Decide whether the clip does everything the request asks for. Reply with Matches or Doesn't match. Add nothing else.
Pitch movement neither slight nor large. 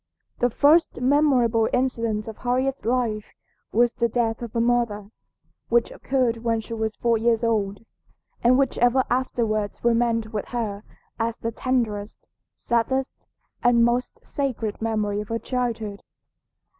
Doesn't match